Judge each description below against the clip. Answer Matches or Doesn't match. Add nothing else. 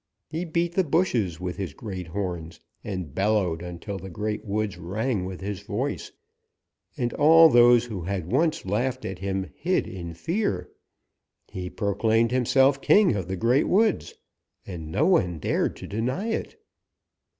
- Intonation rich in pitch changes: Matches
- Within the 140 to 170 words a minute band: Matches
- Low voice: Matches